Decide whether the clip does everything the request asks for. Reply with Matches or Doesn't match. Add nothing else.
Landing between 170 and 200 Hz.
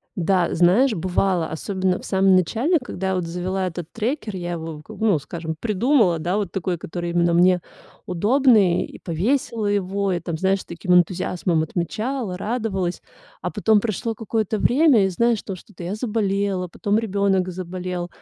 Matches